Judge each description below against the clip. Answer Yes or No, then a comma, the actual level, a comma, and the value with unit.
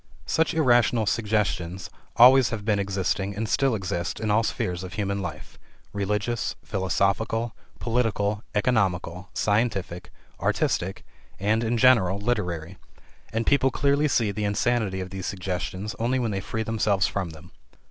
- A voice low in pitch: Yes, low, 105 Hz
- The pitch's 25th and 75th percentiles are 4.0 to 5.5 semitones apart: No, average, 3.2 semitones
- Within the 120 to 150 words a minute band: Yes, average, 140 wpm